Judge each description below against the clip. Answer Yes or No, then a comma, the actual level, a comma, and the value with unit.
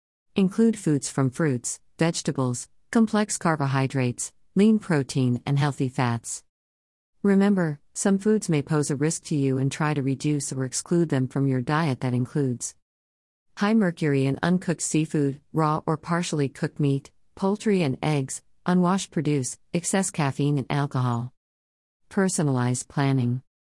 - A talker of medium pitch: Yes, medium, 145 Hz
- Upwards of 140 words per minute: No, slow, 135 wpm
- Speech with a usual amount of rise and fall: Yes, average, 4.7 semitones